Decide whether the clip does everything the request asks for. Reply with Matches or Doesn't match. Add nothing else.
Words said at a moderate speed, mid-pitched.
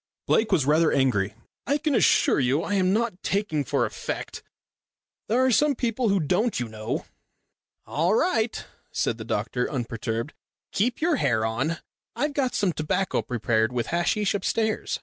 Matches